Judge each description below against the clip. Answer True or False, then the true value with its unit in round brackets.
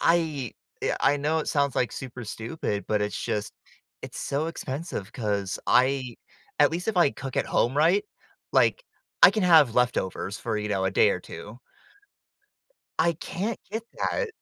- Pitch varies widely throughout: True (6.8 semitones)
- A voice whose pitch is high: False (135 Hz)